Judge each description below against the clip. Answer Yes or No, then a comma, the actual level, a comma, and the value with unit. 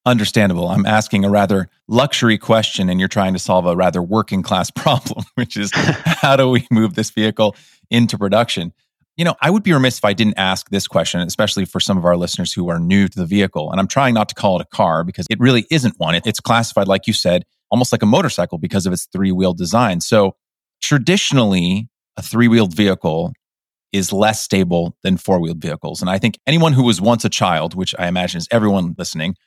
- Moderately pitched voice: No, low, 105 Hz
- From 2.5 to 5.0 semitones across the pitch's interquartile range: Yes, average, 4.1 semitones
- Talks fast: Yes, fast, 220 wpm